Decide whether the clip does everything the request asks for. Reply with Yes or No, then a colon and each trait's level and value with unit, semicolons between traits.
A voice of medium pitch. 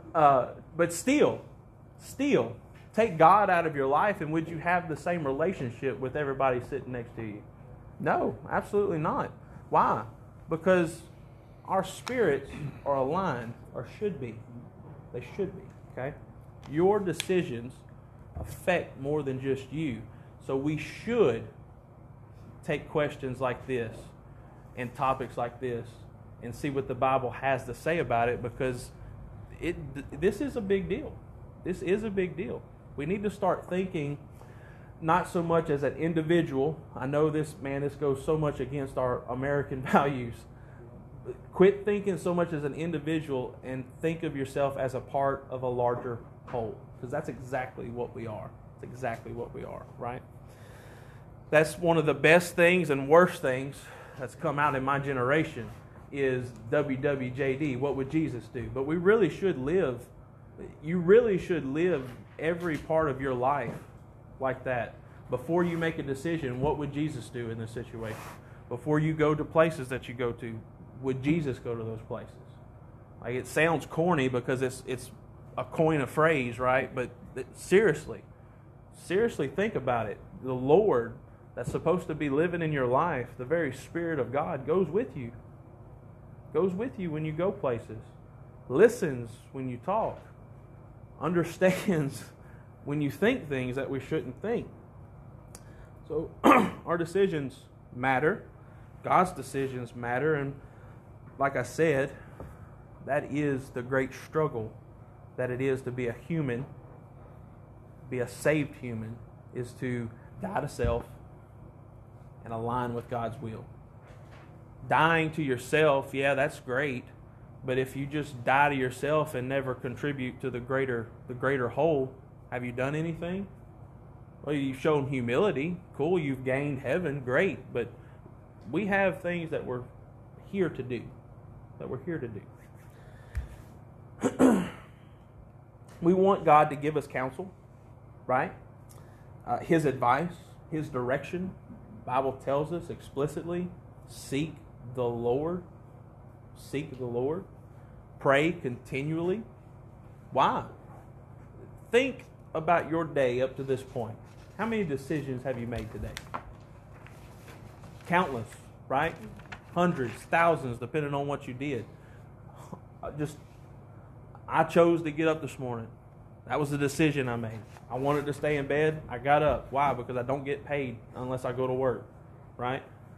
No: low, 130 Hz